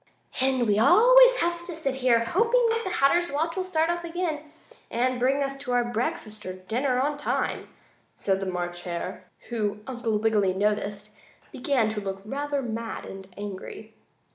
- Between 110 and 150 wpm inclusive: No, average, 165 wpm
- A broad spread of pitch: Yes, wide, 6.7 semitones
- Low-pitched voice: No, very high, 250 Hz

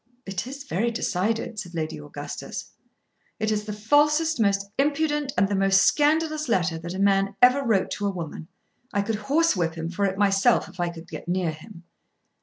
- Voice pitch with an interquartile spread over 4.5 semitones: Yes, wide, 5.6 semitones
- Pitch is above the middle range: Yes, high, 200 Hz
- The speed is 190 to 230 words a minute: Yes, average, 195 wpm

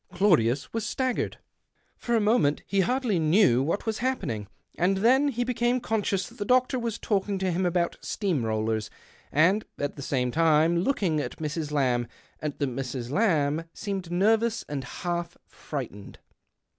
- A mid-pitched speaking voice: Yes, medium, 175 Hz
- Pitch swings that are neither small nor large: No, wide, 7.2 semitones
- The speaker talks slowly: No, average, 160 wpm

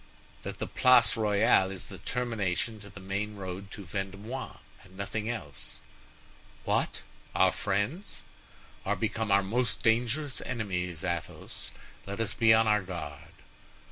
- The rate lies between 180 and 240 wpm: No, average, 140 wpm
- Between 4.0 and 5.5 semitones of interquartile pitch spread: No, average, 2.9 semitones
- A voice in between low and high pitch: No, low, 100 Hz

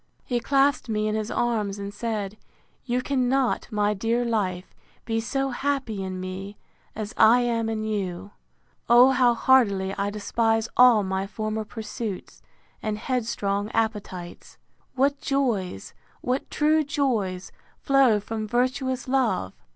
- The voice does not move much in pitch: No, average, 3.7 semitones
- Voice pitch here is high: Yes, high, 225 Hz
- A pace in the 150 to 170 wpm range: No, slow, 135 wpm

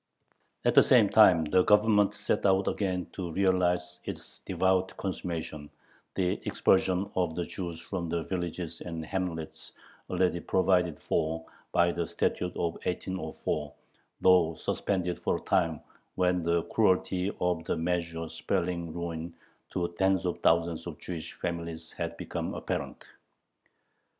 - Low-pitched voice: Yes, very low, 90 Hz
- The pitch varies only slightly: Yes, narrow, 1.8 semitones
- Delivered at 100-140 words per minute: Yes, slow, 135 wpm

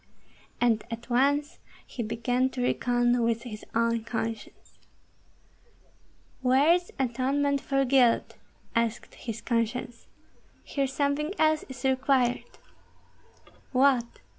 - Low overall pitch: No, very high, 250 Hz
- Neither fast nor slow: No, slow, 105 wpm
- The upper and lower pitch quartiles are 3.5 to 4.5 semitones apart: No, average, 2.7 semitones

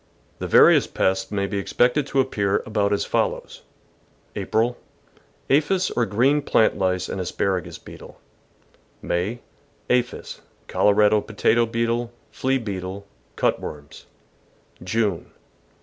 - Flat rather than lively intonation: No, average, 3.8 semitones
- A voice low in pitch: Yes, low, 105 Hz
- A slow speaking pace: Yes, slow, 125 wpm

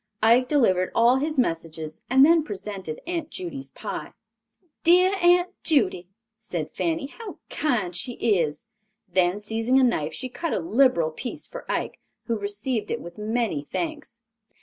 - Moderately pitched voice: No, high, 235 Hz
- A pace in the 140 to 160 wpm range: Yes, average, 150 wpm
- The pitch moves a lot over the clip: Yes, wide, 8.1 semitones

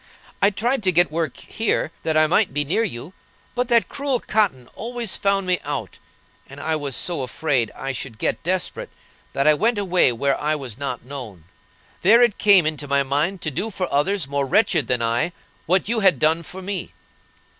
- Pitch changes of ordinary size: No, wide, 6.2 semitones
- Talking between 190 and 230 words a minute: Yes, average, 200 wpm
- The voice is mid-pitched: Yes, medium, 165 Hz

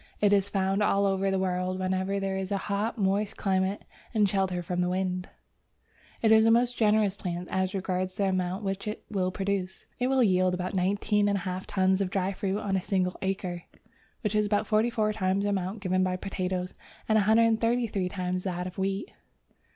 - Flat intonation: Yes, narrow, 1.9 semitones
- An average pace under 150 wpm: No, average, 190 wpm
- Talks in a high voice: Yes, high, 195 Hz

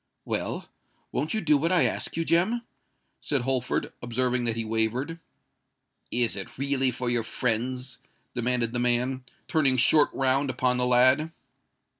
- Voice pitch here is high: No, low, 125 Hz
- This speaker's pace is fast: No, average, 145 wpm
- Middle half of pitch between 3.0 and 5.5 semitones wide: No, narrow, 2.5 semitones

